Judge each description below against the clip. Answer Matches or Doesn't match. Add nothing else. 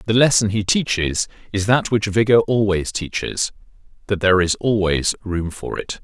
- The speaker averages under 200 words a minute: Matches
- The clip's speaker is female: Doesn't match